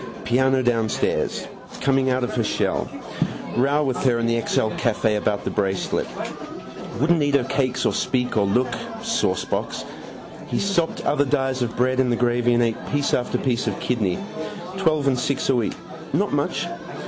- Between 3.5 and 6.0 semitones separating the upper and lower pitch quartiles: No, average, 2.7 semitones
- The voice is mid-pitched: No, low, 125 Hz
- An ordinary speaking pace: Yes, average, 170 wpm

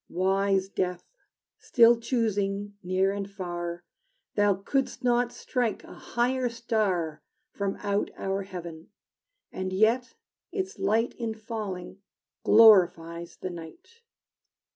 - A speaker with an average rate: No, slow, 110 wpm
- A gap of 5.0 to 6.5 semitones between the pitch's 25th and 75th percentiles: No, average, 3.8 semitones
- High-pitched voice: Yes, high, 200 Hz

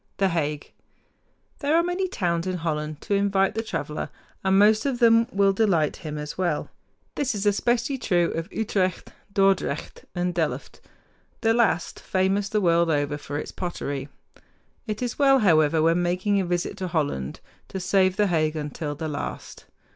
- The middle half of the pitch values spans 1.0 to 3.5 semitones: No, average, 4.6 semitones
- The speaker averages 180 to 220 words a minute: No, average, 170 wpm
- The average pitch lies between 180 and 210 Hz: Yes, medium, 185 Hz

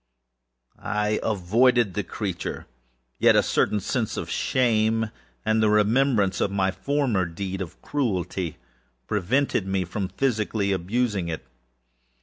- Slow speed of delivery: Yes, slow, 120 wpm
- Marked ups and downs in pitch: No, average, 3.2 semitones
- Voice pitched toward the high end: No, low, 105 Hz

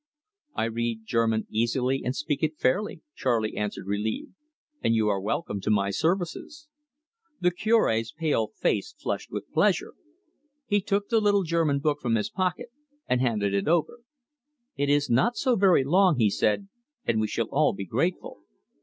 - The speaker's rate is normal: Yes, average, 165 wpm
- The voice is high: No, low, 135 Hz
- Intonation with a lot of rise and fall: Yes, wide, 8.1 semitones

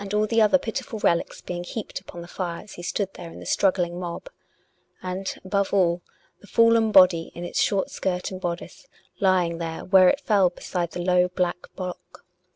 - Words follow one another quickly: No, average, 190 wpm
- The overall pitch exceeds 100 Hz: Yes, medium, 185 Hz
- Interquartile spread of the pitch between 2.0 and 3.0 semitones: Yes, narrow, 2.4 semitones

